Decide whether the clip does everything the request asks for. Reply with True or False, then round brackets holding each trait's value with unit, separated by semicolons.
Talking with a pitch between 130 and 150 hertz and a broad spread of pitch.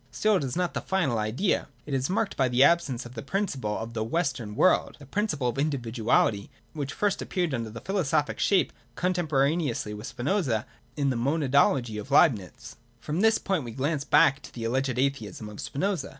True (135 Hz; 6.0 semitones)